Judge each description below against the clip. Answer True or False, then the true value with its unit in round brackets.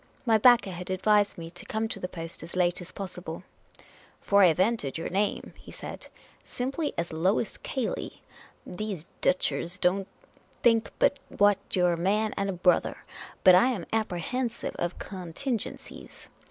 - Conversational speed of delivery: True (175 wpm)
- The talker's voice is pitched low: False (190 Hz)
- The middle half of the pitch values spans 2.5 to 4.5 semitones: True (3.7 semitones)